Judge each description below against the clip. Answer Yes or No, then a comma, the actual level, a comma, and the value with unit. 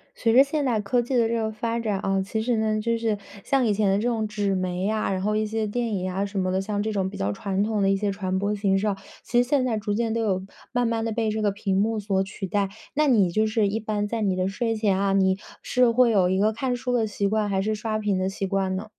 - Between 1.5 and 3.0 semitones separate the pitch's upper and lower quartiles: Yes, narrow, 2.6 semitones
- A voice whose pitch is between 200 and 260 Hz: Yes, high, 210 Hz